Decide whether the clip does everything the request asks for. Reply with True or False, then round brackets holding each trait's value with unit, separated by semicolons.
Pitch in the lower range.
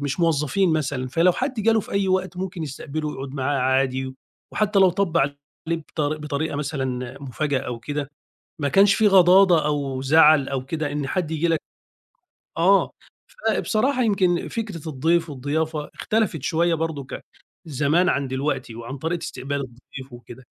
False (150 Hz)